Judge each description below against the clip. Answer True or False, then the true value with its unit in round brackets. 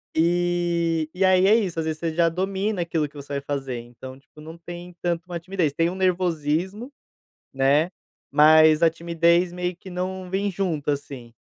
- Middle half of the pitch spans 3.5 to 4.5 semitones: False (3.0 semitones)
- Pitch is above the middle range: False (170 Hz)